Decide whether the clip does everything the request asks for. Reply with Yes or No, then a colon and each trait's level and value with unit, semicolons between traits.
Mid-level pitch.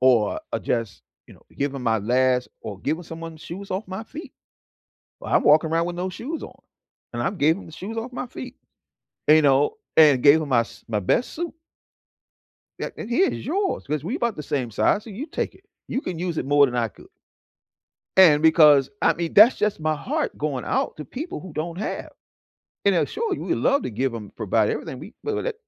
Yes: medium, 160 Hz